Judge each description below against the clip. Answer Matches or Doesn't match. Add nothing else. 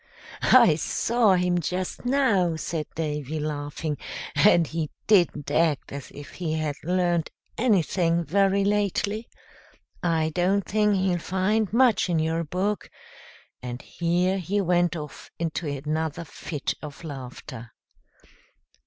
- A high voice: Doesn't match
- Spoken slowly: Matches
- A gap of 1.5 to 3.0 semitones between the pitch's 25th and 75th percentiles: Doesn't match